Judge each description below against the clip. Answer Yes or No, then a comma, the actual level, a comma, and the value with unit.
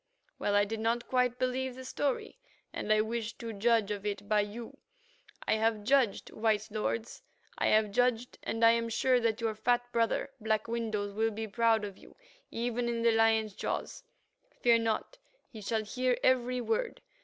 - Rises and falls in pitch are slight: Yes, narrow, 2.1 semitones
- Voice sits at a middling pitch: No, high, 230 Hz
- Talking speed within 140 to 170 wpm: No, average, 180 wpm